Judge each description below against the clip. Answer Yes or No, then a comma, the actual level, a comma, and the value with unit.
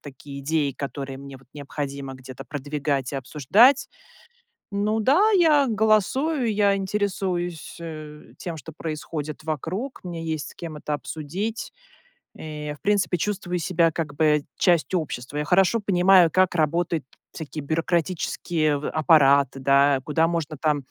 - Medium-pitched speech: Yes, medium, 160 Hz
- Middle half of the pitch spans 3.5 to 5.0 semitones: Yes, average, 4.4 semitones